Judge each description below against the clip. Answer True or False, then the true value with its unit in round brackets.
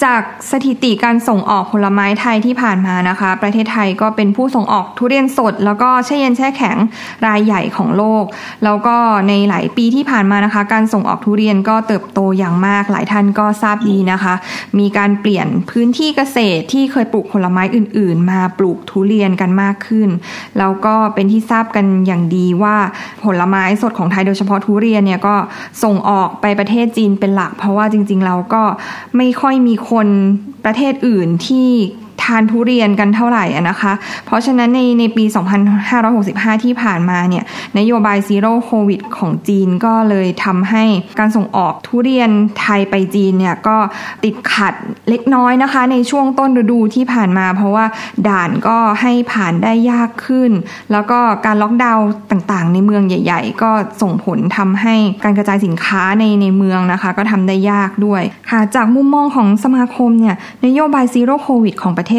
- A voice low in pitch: False (215 Hz)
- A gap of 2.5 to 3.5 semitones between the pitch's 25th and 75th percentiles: True (2.9 semitones)